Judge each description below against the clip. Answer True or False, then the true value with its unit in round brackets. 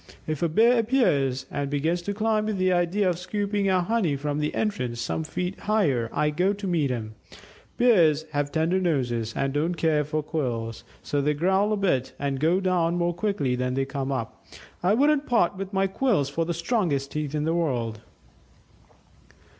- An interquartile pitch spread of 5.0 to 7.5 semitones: True (5.6 semitones)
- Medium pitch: True (165 Hz)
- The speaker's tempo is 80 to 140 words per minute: False (190 wpm)